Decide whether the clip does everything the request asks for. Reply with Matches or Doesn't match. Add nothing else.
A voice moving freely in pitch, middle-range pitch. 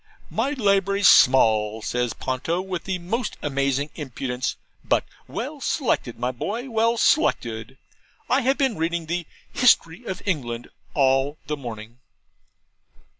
Matches